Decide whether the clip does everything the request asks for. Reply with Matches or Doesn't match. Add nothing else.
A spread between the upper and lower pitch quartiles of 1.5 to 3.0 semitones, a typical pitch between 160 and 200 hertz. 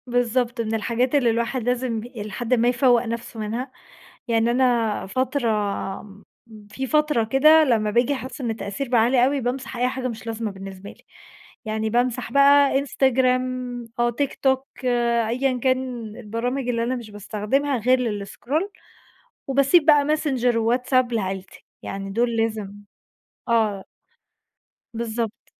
Doesn't match